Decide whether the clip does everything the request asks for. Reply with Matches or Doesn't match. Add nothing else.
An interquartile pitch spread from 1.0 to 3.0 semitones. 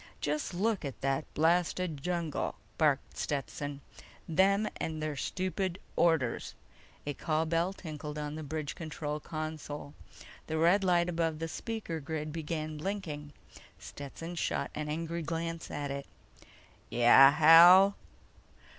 Matches